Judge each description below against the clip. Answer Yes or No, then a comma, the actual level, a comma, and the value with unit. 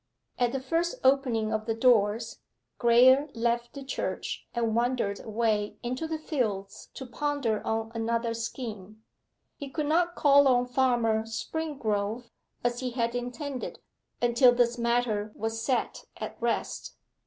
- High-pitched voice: Yes, high, 240 Hz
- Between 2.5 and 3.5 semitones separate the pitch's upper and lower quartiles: Yes, average, 2.8 semitones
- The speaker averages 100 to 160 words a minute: Yes, average, 140 wpm